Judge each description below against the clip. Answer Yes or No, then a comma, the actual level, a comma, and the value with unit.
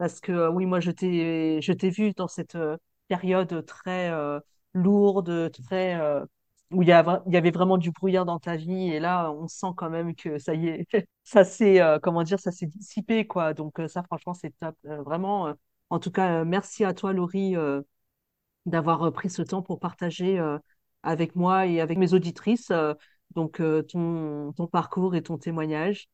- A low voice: No, medium, 175 Hz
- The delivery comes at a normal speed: Yes, average, 195 wpm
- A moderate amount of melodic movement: No, narrow, 2.3 semitones